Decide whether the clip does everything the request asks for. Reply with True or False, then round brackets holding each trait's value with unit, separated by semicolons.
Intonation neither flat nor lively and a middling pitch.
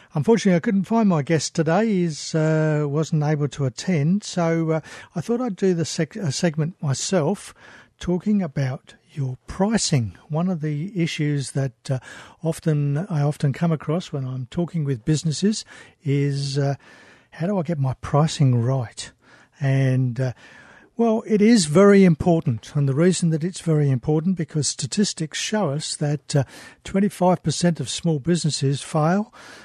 True (4.0 semitones; 160 Hz)